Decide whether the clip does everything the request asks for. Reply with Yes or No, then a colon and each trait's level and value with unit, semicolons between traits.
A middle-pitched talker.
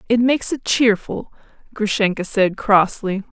No: high, 210 Hz